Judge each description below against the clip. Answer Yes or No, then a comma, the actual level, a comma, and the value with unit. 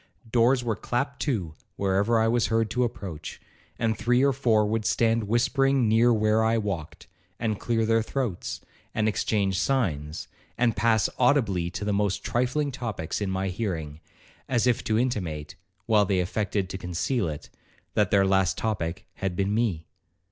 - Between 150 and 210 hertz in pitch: No, low, 110 Hz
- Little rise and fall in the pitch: No, average, 3.7 semitones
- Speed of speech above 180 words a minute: No, average, 165 wpm